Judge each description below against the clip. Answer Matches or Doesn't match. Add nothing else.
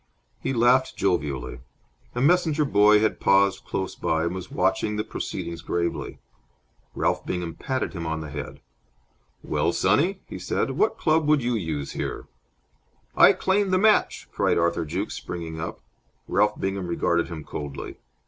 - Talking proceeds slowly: Doesn't match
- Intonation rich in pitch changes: Matches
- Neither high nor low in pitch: Doesn't match